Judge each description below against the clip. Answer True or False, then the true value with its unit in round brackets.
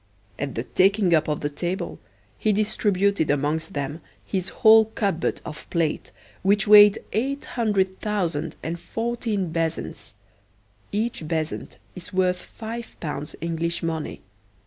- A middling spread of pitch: True (4.7 semitones)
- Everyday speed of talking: False (130 wpm)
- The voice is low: False (185 Hz)